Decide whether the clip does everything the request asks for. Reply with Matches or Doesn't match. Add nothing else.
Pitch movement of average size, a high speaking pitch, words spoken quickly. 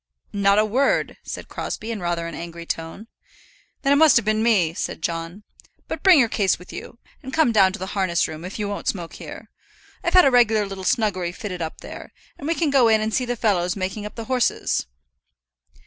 Matches